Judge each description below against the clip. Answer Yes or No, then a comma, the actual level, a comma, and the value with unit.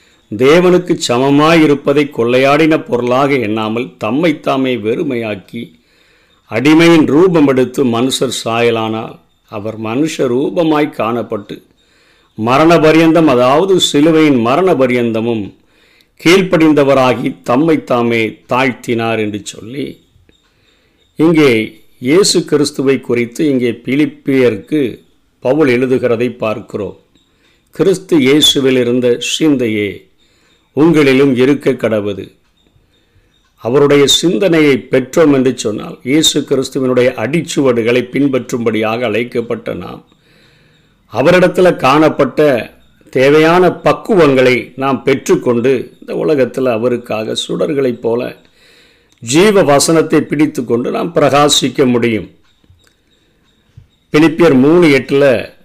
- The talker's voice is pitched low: Yes, low, 130 Hz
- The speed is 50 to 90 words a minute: Yes, average, 80 wpm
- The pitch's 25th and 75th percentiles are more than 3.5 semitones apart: Yes, average, 4.5 semitones